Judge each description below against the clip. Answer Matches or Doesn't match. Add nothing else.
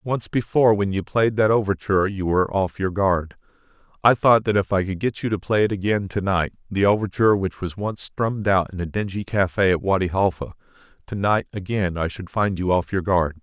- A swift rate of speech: Matches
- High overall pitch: Doesn't match